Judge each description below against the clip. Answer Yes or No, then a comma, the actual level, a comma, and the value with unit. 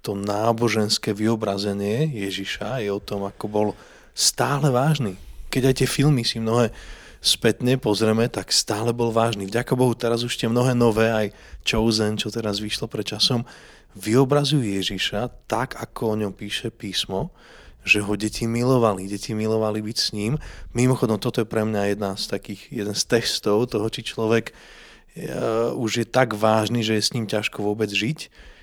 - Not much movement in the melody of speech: Yes, narrow, 2.3 semitones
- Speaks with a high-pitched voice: No, low, 110 Hz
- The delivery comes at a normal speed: No, fast, 170 wpm